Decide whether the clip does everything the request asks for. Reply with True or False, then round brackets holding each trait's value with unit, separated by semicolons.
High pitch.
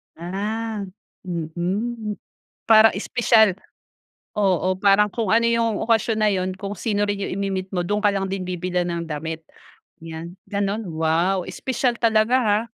True (200 Hz)